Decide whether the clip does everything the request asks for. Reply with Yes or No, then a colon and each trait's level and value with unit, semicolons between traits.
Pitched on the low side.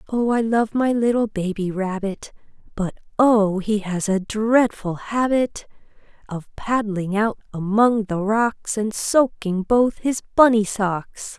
No: high, 215 Hz